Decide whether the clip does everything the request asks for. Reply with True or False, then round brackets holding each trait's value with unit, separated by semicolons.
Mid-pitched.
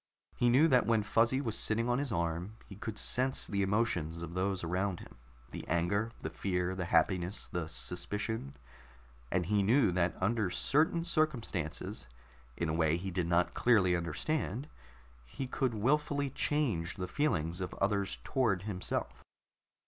False (100 Hz)